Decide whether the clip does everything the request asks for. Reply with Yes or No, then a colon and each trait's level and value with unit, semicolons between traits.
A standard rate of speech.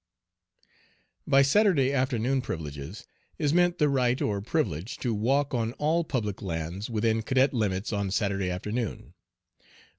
No: slow, 130 wpm